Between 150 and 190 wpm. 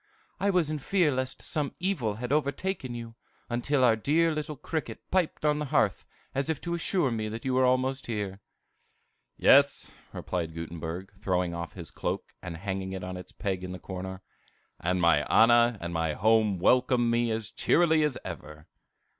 Yes: average, 180 wpm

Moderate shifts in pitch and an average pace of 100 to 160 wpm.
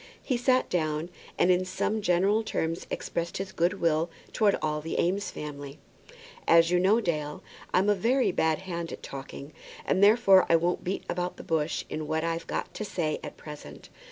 No: average, 3.8 semitones; average, 185 wpm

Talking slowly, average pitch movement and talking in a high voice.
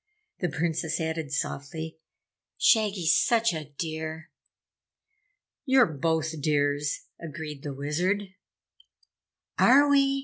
No: slow, 95 wpm; average, 4.5 semitones; medium, 160 Hz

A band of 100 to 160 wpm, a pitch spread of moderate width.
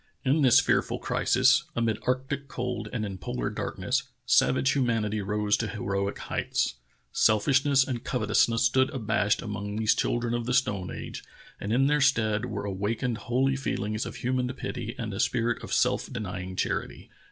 No: average, 170 wpm; average, 3.4 semitones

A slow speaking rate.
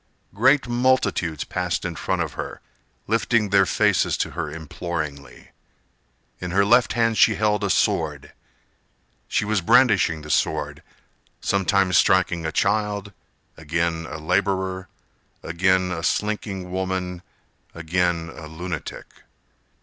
Yes: slow, 120 wpm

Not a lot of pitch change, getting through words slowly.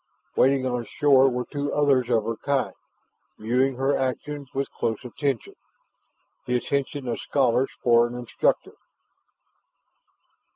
Yes: narrow, 2.3 semitones; slow, 125 wpm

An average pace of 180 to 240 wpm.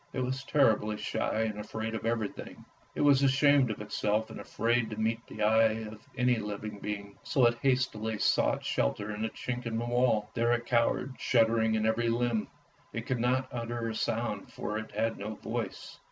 Yes: average, 195 wpm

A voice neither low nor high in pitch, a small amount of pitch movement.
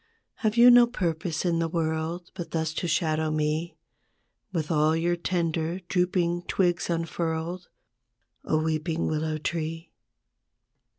Yes: medium, 165 Hz; narrow, 1.7 semitones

